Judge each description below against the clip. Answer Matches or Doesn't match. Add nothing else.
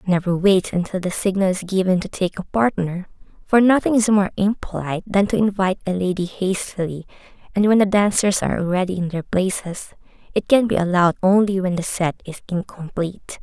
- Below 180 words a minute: Doesn't match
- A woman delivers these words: Matches